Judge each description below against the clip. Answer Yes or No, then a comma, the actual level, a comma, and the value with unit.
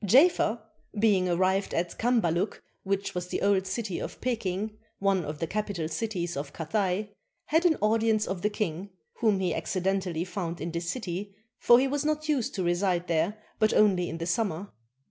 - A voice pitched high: Yes, high, 195 Hz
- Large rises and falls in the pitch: No, average, 3.7 semitones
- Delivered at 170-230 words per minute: Yes, average, 180 wpm